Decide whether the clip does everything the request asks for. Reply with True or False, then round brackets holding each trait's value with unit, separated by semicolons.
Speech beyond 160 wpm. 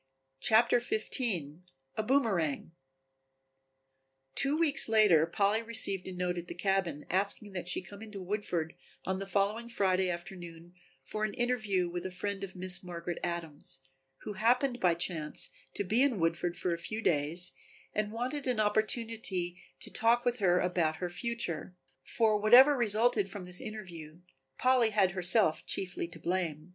False (155 wpm)